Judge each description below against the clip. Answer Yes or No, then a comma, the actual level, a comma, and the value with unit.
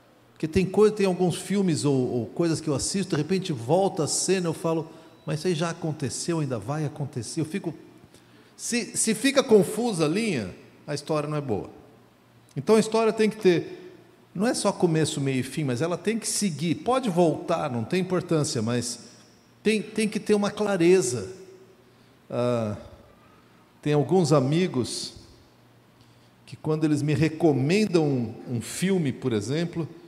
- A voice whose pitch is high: No, medium, 165 Hz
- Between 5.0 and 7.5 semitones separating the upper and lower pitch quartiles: Yes, average, 5.3 semitones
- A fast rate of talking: No, average, 170 wpm